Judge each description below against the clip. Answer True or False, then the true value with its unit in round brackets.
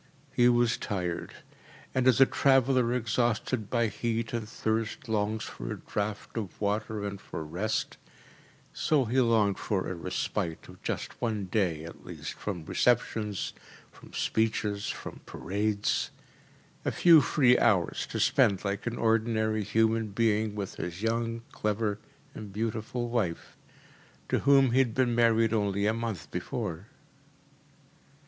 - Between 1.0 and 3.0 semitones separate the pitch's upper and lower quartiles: True (2.5 semitones)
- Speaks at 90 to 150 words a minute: True (140 wpm)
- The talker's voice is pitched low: True (110 Hz)